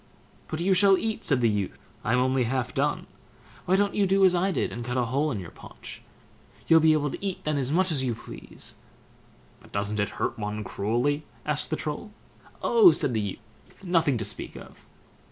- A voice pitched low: No, medium, 145 Hz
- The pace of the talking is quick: Yes, fast, 210 wpm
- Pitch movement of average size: No, wide, 7.4 semitones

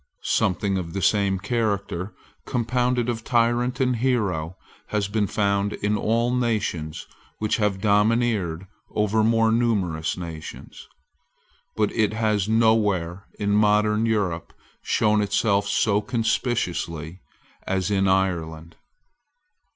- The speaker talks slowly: Yes, slow, 110 wpm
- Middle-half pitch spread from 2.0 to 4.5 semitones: Yes, average, 2.9 semitones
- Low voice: Yes, low, 105 Hz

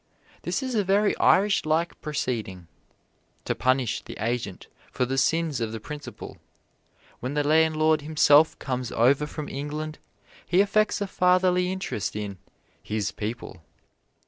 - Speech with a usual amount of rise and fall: No, wide, 6.1 semitones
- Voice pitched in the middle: Yes, medium, 150 Hz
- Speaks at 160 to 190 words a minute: No, average, 140 wpm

